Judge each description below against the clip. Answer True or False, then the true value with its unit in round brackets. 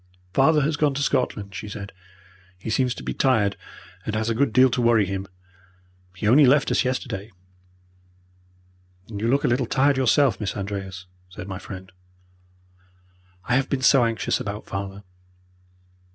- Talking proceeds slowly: False (165 wpm)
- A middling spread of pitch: True (4.7 semitones)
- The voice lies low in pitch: True (115 Hz)